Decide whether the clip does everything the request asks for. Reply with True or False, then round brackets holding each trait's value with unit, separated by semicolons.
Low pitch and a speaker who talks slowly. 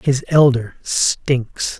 True (130 Hz; 100 wpm)